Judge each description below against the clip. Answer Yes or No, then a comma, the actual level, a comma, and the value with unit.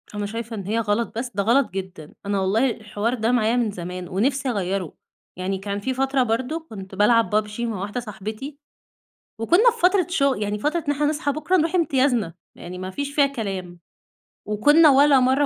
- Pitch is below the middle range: No, high, 230 Hz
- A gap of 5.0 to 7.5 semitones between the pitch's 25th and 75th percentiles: Yes, wide, 5.6 semitones